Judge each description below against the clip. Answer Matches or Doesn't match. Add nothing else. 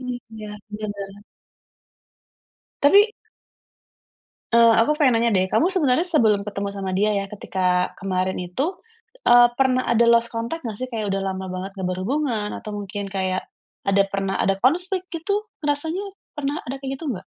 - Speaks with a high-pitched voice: Matches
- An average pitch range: Doesn't match